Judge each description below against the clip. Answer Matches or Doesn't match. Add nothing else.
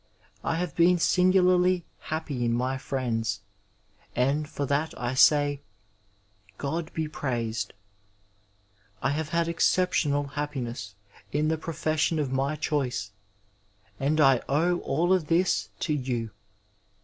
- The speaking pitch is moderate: Matches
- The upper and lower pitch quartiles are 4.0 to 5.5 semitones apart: Matches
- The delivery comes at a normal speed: Doesn't match